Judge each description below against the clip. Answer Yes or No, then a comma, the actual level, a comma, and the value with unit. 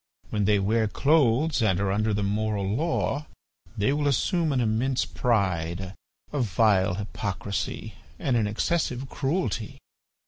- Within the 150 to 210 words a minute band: No, slow, 135 wpm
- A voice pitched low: Yes, low, 110 Hz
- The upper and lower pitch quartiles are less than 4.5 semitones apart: No, average, 5.2 semitones